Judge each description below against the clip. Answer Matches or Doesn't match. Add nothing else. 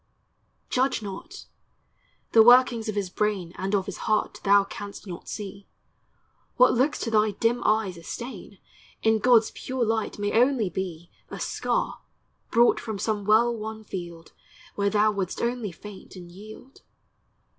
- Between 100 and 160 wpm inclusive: Matches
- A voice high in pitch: Matches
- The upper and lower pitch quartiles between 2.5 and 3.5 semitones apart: Matches